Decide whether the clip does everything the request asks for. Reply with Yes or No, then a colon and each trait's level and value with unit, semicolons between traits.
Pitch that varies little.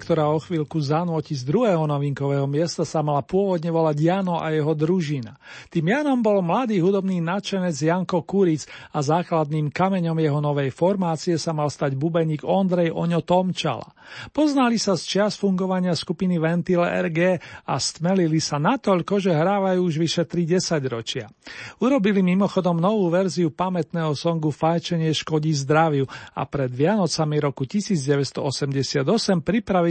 No: average, 3.3 semitones